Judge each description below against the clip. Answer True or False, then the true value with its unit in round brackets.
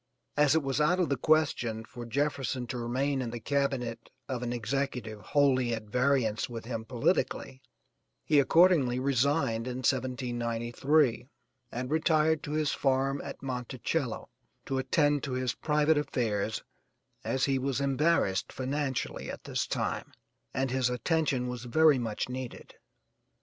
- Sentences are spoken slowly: False (145 wpm)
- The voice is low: True (130 Hz)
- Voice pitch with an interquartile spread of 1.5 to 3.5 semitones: True (3.0 semitones)